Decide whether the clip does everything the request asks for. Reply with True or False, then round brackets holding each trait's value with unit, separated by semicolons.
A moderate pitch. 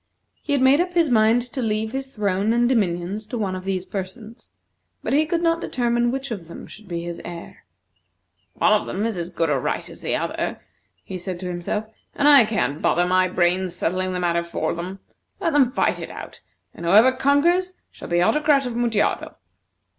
False (215 Hz)